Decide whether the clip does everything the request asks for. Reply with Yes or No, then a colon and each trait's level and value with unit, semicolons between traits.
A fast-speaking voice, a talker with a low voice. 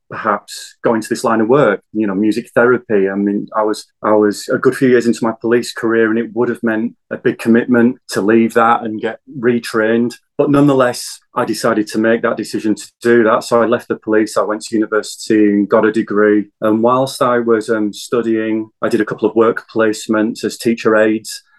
Yes: fast, 220 wpm; low, 115 Hz